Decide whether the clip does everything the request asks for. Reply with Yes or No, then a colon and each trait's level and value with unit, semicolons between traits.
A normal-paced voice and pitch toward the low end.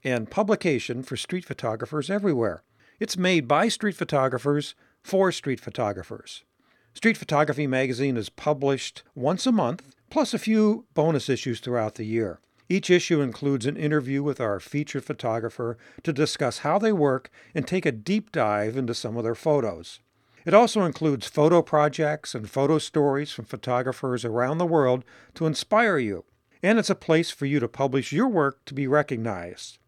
No: average, 165 wpm; medium, 145 Hz